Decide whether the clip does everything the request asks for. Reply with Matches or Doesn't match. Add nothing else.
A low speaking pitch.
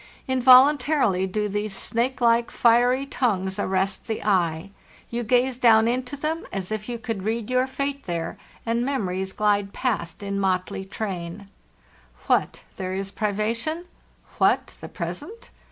Doesn't match